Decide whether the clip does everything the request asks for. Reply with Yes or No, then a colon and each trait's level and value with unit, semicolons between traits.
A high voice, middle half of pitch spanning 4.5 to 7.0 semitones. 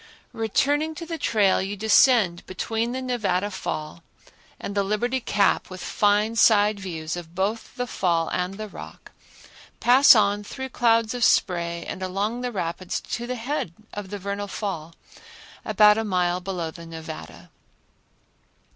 No: high, 205 Hz; average, 4.0 semitones